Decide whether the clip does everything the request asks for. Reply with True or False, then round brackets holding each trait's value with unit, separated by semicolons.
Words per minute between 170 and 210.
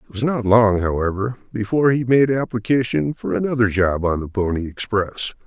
True (175 wpm)